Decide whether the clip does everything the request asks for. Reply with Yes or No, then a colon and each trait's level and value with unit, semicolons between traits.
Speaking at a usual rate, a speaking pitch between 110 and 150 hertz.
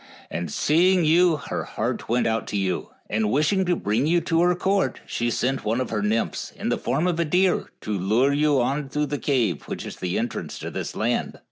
No: fast, 225 wpm; medium, 140 Hz